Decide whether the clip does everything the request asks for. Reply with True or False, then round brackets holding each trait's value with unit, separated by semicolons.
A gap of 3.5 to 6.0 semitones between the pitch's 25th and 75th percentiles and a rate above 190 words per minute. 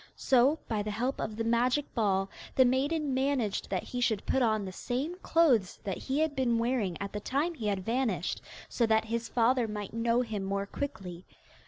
True (4.0 semitones; 200 wpm)